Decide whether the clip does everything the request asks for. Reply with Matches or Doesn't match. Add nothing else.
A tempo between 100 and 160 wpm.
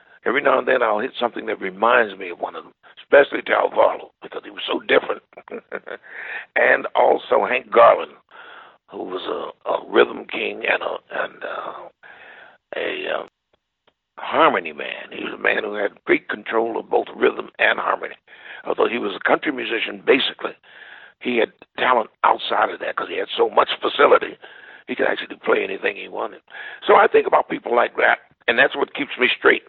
Doesn't match